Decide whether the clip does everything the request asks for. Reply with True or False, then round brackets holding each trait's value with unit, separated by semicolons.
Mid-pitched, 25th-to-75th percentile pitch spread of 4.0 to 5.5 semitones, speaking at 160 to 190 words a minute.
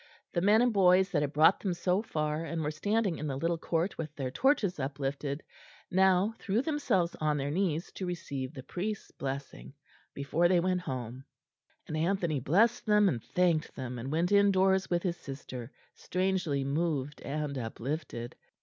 True (165 Hz; 5.2 semitones; 170 wpm)